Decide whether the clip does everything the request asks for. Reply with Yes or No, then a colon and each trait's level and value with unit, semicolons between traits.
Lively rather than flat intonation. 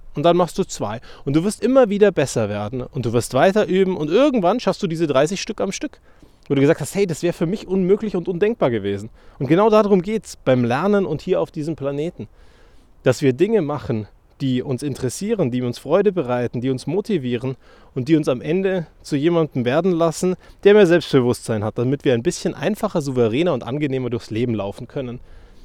Yes: wide, 7.3 semitones